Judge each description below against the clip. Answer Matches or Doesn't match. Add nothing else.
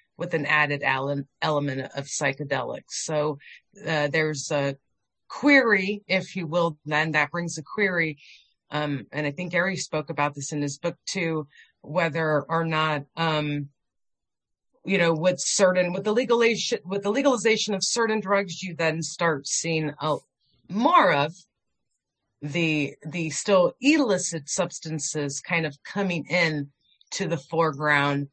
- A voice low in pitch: Doesn't match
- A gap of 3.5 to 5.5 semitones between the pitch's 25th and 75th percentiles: Matches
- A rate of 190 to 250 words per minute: Doesn't match